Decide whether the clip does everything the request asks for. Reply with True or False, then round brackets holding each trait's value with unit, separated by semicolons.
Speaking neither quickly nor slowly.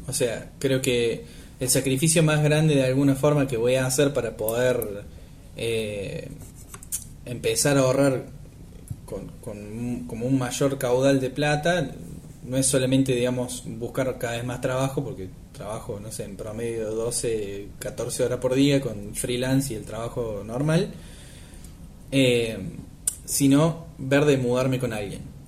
True (150 wpm)